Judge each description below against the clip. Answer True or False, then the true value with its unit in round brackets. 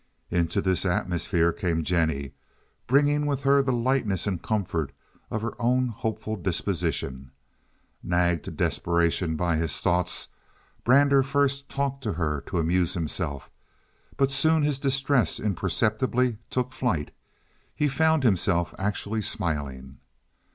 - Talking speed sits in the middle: False (125 wpm)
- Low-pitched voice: True (100 Hz)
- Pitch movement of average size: False (7.7 semitones)